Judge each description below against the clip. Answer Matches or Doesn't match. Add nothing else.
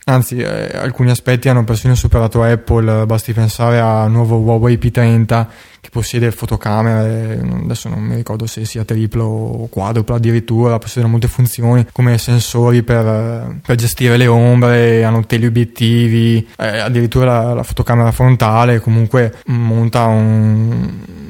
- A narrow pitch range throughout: Matches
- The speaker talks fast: Doesn't match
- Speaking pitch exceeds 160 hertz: Doesn't match